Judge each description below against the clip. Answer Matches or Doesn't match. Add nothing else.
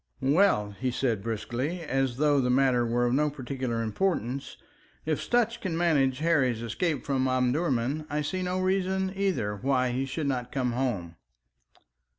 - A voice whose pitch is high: Doesn't match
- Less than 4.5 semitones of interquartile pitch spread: Doesn't match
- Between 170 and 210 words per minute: Doesn't match